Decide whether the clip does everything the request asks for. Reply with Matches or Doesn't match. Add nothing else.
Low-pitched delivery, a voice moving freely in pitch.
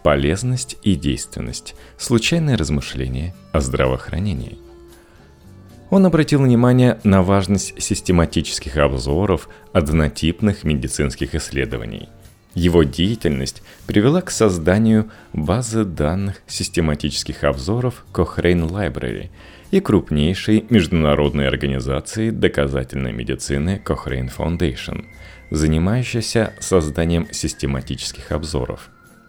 Matches